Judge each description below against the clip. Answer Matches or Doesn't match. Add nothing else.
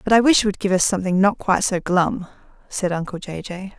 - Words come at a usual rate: Doesn't match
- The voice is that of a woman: Matches